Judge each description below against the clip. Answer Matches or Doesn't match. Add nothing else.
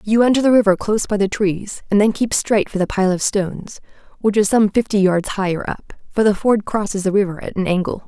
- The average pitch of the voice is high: Matches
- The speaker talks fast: Matches